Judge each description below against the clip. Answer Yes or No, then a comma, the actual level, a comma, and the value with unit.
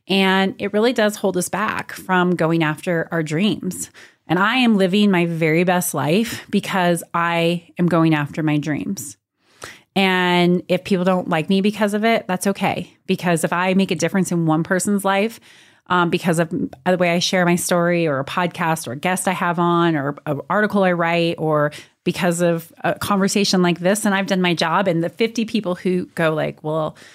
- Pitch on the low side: No, medium, 180 Hz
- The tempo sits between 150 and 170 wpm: No, average, 200 wpm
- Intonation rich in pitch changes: No, narrow, 2.5 semitones